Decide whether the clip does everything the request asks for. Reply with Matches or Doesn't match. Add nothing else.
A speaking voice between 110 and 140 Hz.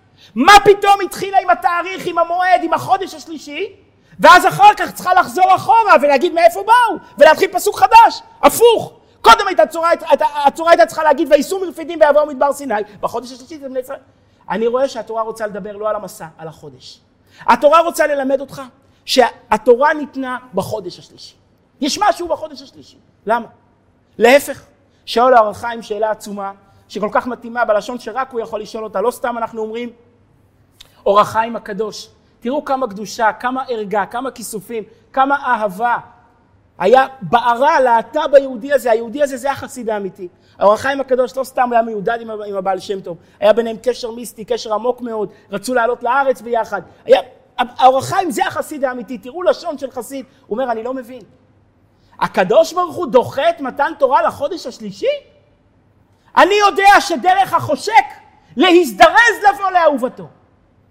Doesn't match